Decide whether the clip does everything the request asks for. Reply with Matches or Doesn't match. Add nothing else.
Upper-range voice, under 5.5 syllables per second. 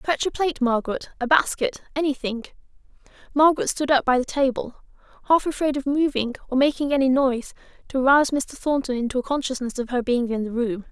Doesn't match